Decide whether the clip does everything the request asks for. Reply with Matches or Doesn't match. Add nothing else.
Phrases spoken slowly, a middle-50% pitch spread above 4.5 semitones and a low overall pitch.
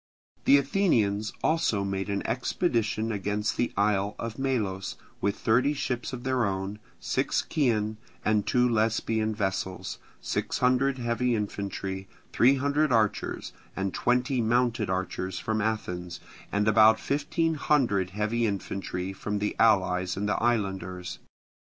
Doesn't match